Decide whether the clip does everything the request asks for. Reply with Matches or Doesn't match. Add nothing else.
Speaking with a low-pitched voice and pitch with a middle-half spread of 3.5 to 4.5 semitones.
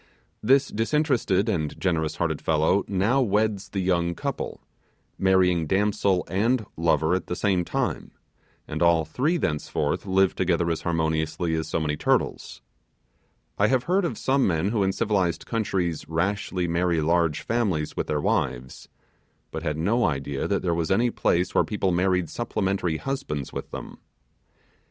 Matches